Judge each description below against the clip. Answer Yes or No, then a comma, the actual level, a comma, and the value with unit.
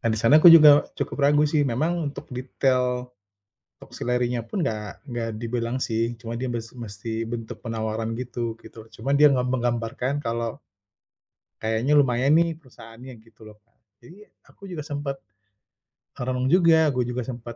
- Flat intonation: No, average, 3.6 semitones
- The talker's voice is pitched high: No, low, 125 Hz